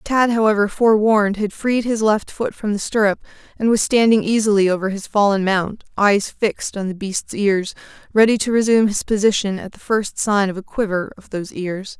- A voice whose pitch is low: No, high, 205 Hz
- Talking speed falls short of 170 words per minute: No, average, 200 wpm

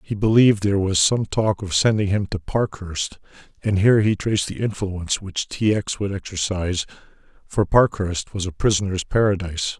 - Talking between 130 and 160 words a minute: No, average, 170 wpm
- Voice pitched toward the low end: Yes, low, 100 Hz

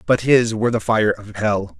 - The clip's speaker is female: No, male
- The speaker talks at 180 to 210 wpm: No, fast, 235 wpm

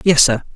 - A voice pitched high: No, low, 135 Hz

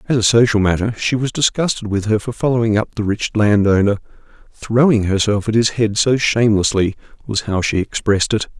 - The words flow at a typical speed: Yes, average, 180 wpm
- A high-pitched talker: No, low, 110 Hz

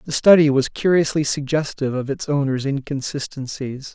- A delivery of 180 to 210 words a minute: No, slow, 135 wpm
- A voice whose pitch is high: No, medium, 140 Hz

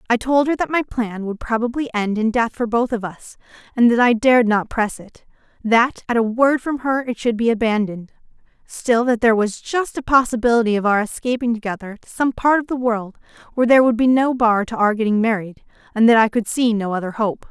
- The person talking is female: Yes, female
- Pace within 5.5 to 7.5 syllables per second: Yes, 5.7 syllables/s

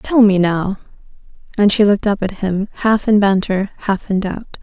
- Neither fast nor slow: Yes, average, 195 wpm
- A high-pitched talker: Yes, high, 200 Hz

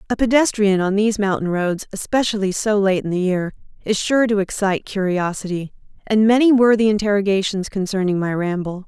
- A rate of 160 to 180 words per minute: Yes, average, 170 wpm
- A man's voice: No, female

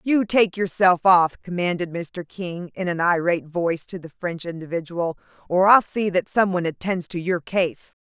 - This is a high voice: No, medium, 180 Hz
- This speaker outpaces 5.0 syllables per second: No, 4.9 syllables/s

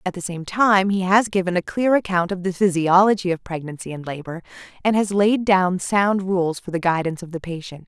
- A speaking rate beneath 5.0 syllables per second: No, 5.4 syllables/s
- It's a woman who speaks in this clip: Yes, female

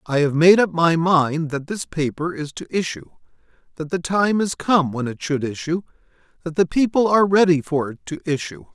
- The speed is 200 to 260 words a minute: Yes, fast, 205 wpm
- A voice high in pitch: No, medium, 165 Hz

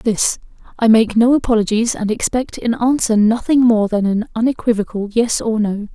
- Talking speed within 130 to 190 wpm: Yes, average, 170 wpm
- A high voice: Yes, high, 225 Hz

